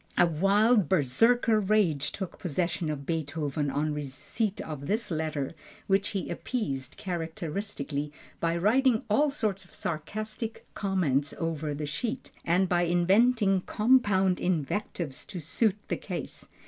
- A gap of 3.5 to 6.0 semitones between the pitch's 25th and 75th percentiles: Yes, wide, 5.6 semitones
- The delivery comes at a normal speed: No, slow, 130 wpm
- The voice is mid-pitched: Yes, medium, 180 Hz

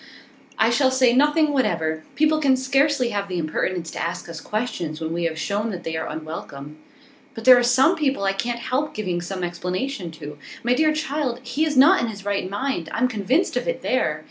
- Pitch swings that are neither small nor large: No, wide, 7.6 semitones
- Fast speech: Yes, fast, 210 wpm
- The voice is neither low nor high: No, high, 225 Hz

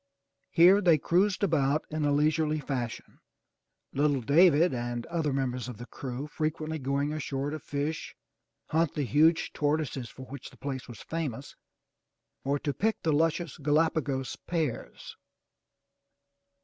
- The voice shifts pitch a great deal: No, average, 2.9 semitones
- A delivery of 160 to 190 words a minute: No, average, 140 wpm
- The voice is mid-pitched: Yes, medium, 150 Hz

